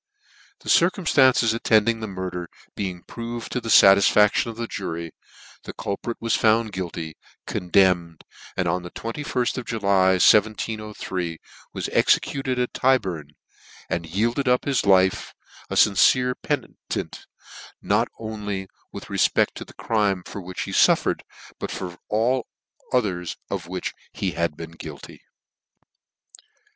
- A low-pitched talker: Yes, low, 100 Hz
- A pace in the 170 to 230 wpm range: No, slow, 135 wpm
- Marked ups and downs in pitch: No, average, 4.3 semitones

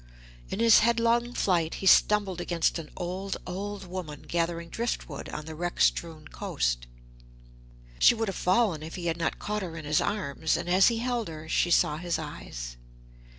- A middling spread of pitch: Yes, average, 4.4 semitones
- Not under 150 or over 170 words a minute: No, average, 185 wpm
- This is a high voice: No, medium, 175 Hz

